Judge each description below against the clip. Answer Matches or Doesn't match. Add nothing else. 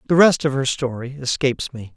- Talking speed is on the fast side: Matches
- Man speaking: Matches